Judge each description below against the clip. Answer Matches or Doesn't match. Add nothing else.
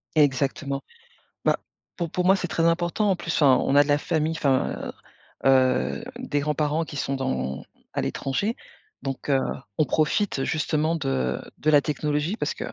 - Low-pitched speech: Doesn't match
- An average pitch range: Matches